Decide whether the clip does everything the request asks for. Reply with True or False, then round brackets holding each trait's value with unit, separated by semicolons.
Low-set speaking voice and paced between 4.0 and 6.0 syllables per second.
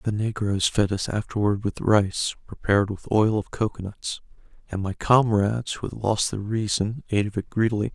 True (105 Hz; 5.2 syllables/s)